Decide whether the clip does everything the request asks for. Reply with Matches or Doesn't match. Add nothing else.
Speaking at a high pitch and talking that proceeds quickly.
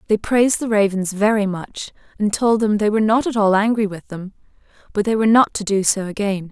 Matches